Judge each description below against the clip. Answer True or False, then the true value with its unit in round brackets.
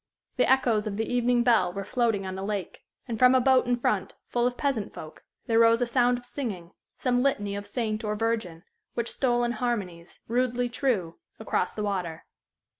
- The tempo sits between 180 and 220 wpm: True (195 wpm)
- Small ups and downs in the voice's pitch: False (3.4 semitones)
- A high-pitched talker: True (230 Hz)